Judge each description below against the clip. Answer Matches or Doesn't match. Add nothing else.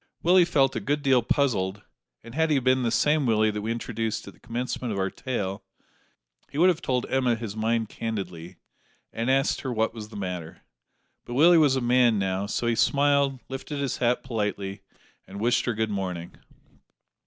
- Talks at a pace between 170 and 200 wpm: Matches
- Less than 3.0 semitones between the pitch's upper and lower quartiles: Doesn't match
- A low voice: Matches